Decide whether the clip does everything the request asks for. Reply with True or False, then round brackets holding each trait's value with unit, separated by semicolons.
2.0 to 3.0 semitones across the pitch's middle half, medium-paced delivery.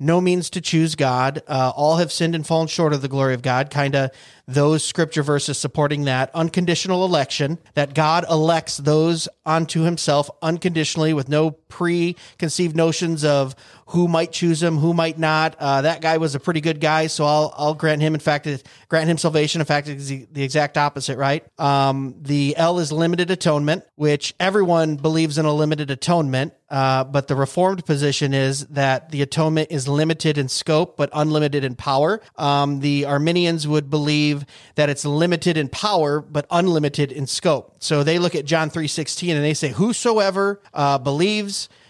True (2.5 semitones; 185 wpm)